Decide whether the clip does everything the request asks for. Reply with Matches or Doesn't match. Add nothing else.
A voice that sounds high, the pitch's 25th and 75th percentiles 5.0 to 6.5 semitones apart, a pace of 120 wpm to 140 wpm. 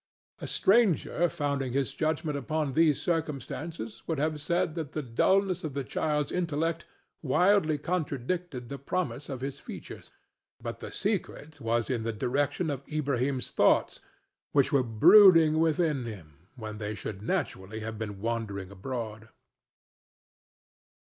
Doesn't match